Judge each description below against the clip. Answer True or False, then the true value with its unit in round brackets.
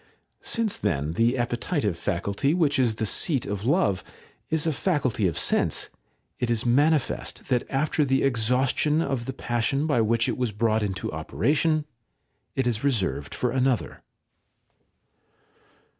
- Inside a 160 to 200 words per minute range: False (145 wpm)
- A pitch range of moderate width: True (4.6 semitones)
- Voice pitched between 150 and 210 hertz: False (125 Hz)